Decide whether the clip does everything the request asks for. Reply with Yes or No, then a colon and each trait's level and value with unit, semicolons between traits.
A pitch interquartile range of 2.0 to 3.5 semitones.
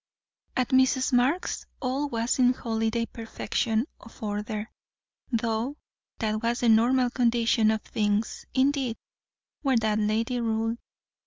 Yes: narrow, 2.5 semitones